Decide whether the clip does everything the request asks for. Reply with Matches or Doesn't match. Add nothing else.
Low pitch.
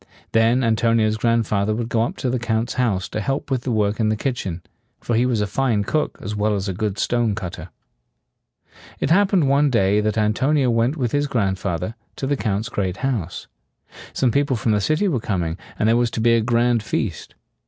Matches